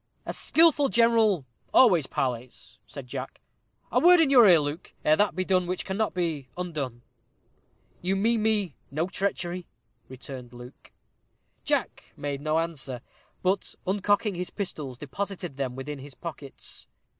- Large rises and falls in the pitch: Yes, wide, 6.5 semitones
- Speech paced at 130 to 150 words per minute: Yes, average, 145 wpm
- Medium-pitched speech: Yes, medium, 175 Hz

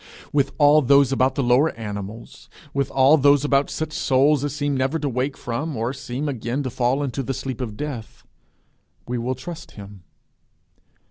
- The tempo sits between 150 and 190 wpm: Yes, average, 180 wpm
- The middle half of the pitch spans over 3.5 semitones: No, average, 2.9 semitones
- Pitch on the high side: No, low, 135 Hz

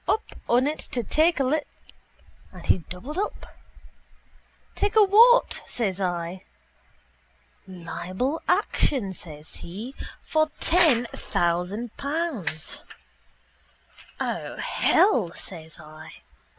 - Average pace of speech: No, slow, 105 wpm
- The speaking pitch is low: No, high, 235 Hz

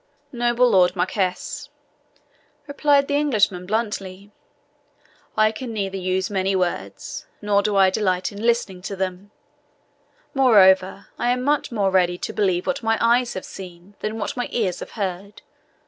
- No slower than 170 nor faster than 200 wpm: No, average, 150 wpm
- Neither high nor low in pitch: No, high, 200 Hz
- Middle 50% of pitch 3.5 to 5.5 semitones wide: Yes, average, 4.0 semitones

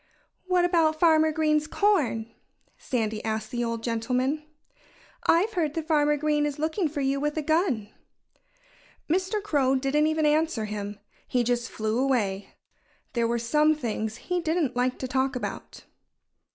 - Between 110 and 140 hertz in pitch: No, very high, 285 Hz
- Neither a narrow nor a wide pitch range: Yes, average, 5.0 semitones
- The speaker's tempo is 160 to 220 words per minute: No, average, 150 wpm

